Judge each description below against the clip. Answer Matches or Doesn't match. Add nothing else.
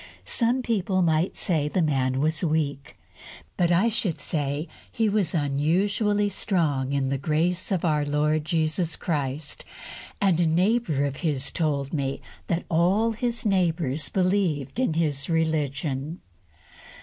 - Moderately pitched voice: Matches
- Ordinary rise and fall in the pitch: Matches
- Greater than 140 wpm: Doesn't match